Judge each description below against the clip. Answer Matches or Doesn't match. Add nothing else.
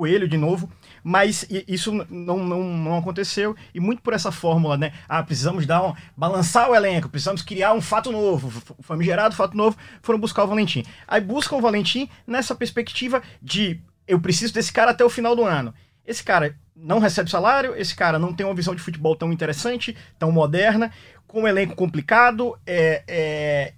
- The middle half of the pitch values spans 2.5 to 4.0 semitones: Doesn't match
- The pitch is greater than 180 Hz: Matches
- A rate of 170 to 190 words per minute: Matches